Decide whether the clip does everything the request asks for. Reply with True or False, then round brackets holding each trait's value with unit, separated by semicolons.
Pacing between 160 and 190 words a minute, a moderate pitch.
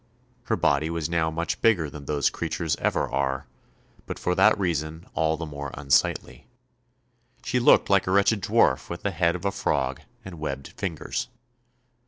False (170 wpm; 80 Hz)